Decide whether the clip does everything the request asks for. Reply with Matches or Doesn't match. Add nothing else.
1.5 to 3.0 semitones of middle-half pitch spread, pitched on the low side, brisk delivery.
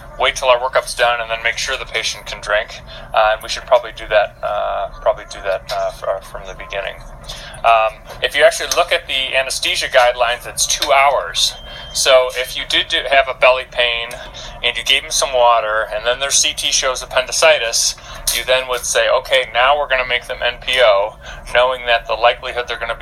Matches